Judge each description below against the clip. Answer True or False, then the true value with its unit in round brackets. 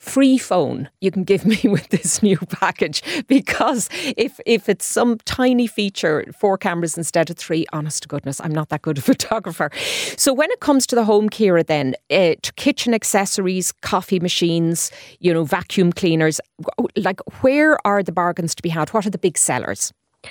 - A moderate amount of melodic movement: False (6.3 semitones)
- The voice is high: True (195 Hz)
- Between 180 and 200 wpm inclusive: True (190 wpm)